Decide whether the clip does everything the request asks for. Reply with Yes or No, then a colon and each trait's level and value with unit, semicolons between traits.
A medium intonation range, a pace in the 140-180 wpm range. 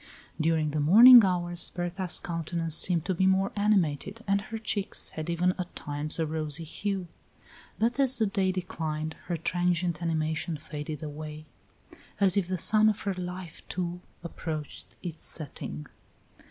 Yes: average, 3.4 semitones; average, 155 wpm